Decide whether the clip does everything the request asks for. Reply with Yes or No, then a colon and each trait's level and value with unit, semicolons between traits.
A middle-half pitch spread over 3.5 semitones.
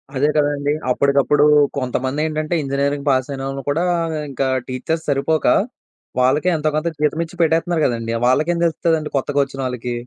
No: narrow, 2.5 semitones